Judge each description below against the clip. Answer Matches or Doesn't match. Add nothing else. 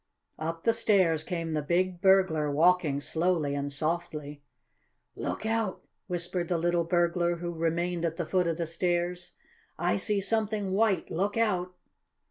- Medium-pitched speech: Matches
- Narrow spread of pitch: Matches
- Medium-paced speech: Matches